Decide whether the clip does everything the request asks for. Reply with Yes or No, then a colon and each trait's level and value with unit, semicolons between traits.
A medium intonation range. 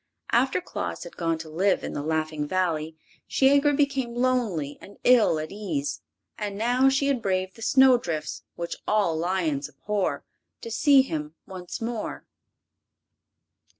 No: wide, 7.6 semitones